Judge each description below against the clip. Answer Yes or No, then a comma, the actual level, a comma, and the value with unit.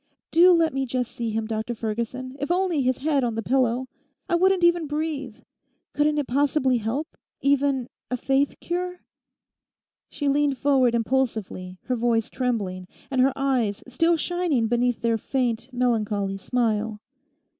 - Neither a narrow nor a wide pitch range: Yes, average, 4.0 semitones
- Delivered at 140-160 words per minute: Yes, average, 145 wpm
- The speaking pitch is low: No, very high, 255 Hz